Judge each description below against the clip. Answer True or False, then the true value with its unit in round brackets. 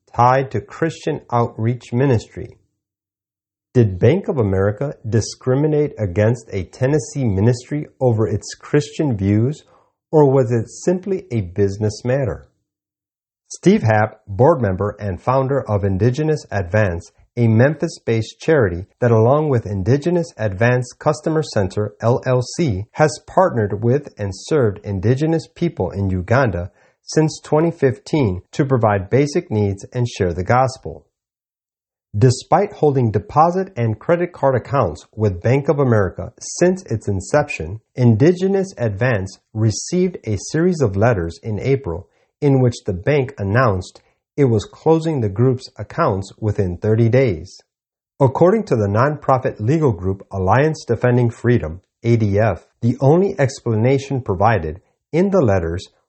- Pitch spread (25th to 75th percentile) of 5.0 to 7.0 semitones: True (5.3 semitones)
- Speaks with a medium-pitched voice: False (120 Hz)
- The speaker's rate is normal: False (125 wpm)